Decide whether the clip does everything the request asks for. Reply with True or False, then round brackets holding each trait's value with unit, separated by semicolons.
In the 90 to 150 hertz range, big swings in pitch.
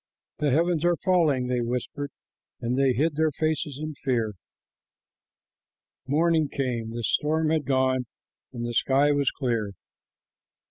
False (140 Hz; 3.8 semitones)